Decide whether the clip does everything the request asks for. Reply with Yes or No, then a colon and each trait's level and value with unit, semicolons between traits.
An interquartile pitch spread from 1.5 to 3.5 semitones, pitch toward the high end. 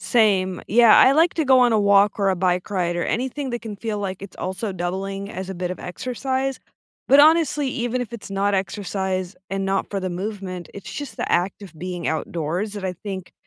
No: average, 4.2 semitones; high, 195 Hz